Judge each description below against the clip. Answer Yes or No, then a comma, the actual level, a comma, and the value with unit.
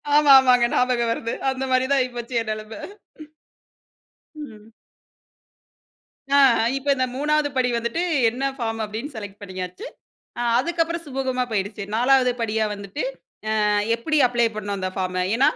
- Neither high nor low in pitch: No, high, 240 Hz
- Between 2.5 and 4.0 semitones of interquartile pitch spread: Yes, average, 3.7 semitones